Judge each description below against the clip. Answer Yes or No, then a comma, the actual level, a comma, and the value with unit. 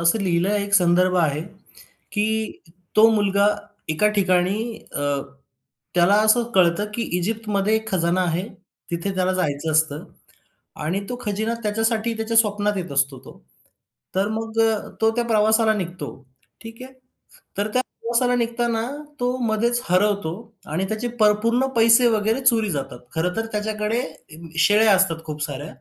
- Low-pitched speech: No, high, 210 Hz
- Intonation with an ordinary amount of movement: Yes, average, 3.9 semitones